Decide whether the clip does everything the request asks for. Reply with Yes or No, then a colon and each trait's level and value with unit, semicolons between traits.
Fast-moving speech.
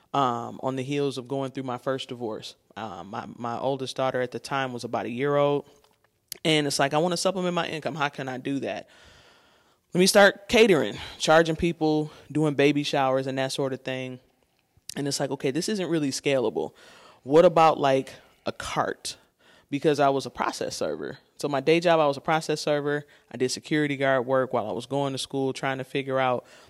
Yes: fast, 215 wpm